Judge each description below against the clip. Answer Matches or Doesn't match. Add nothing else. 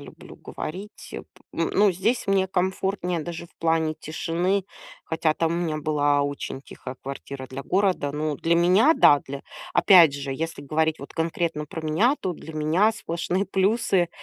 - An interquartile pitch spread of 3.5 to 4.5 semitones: Matches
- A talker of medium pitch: Matches